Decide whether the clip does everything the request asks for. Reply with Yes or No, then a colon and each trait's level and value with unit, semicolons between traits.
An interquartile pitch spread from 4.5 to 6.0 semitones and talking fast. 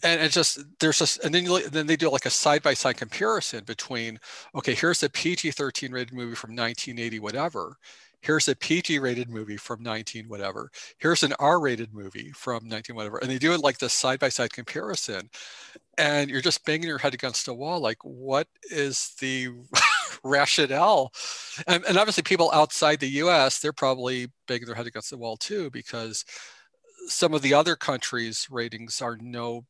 No: average, 4.9 semitones; average, 185 wpm